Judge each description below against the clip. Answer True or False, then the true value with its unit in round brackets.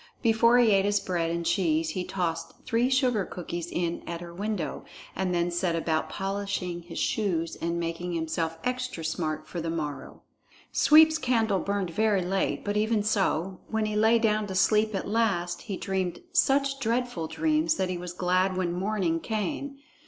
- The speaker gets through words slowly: False (175 wpm)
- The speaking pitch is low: False (190 Hz)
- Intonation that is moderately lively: True (4.3 semitones)